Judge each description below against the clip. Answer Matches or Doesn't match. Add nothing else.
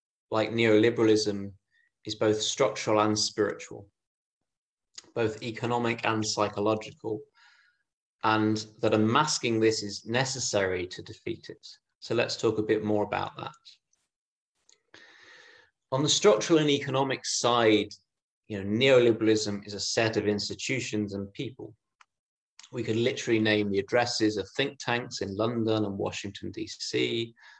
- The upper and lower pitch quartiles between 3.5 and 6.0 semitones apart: Doesn't match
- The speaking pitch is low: Matches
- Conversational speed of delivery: Doesn't match